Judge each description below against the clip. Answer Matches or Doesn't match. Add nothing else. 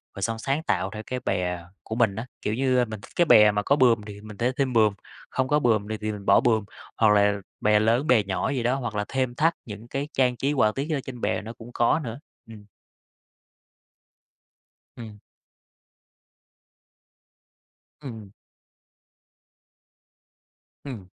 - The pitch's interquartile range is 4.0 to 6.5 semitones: Doesn't match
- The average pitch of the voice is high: Doesn't match